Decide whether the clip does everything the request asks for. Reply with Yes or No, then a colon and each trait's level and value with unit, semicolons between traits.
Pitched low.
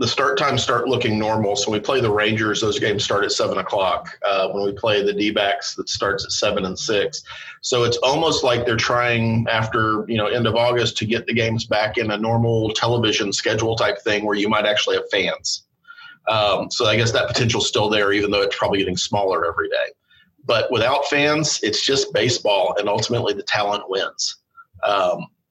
Yes: low, 115 Hz